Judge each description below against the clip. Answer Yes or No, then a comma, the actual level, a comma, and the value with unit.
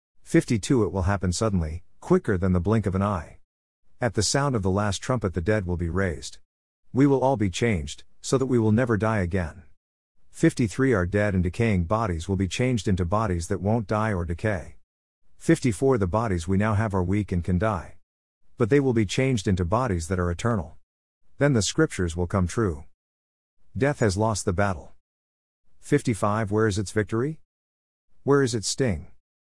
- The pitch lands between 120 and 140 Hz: No, low, 100 Hz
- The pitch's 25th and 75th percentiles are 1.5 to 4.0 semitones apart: No, average, 4.5 semitones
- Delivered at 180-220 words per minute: Yes, average, 190 wpm